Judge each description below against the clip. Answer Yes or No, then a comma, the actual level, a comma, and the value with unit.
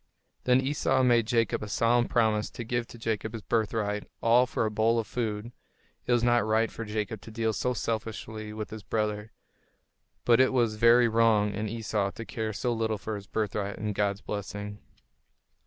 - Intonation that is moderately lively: No, narrow, 1.7 semitones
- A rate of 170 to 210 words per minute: Yes, average, 190 wpm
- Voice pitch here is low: Yes, low, 110 Hz